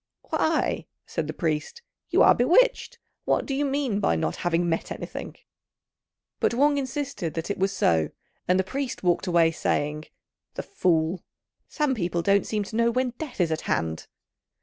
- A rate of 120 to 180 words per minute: Yes, average, 170 wpm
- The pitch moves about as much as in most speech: No, wide, 8.5 semitones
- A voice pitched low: No, high, 190 Hz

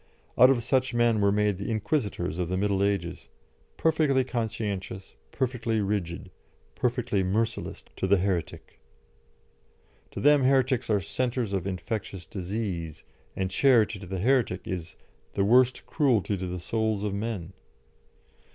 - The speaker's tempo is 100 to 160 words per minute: Yes, average, 140 wpm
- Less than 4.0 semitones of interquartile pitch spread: No, average, 4.3 semitones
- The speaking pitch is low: Yes, low, 105 Hz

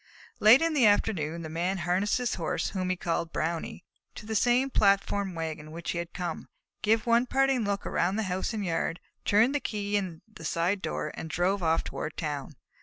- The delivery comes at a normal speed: No, fast, 210 wpm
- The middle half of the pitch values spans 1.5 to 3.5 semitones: No, average, 4.4 semitones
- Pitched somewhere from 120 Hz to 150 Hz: No, high, 190 Hz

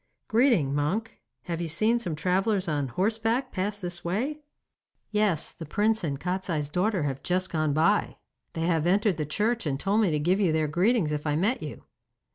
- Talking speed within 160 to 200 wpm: Yes, average, 190 wpm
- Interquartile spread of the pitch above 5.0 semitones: Yes, wide, 5.5 semitones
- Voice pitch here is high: No, medium, 180 Hz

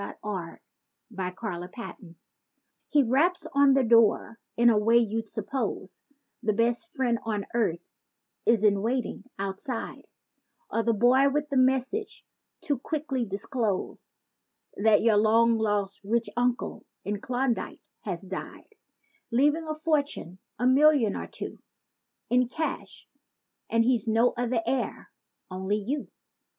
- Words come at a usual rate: No, slow, 125 wpm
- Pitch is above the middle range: Yes, high, 235 Hz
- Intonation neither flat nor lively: Yes, average, 4.0 semitones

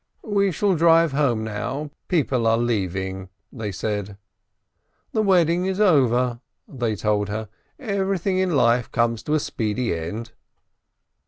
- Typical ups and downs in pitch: No, wide, 7.8 semitones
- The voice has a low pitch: Yes, low, 125 Hz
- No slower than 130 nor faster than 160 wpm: Yes, slow, 135 wpm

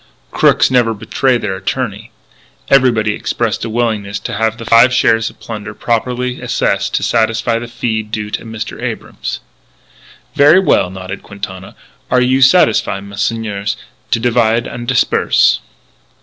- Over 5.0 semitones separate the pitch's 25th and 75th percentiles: No, narrow, 2.4 semitones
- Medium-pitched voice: No, low, 115 Hz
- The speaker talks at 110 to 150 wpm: Yes, average, 140 wpm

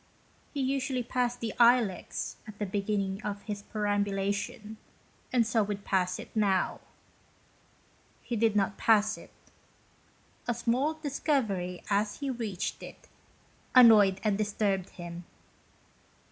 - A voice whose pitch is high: Yes, high, 210 Hz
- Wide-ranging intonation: No, average, 3.2 semitones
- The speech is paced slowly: Yes, slow, 125 wpm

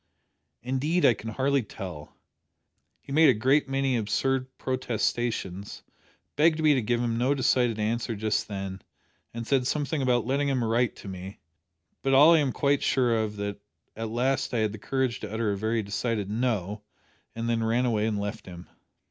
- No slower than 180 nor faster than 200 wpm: Yes, average, 185 wpm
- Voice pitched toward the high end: No, low, 120 Hz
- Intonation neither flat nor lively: Yes, average, 3.9 semitones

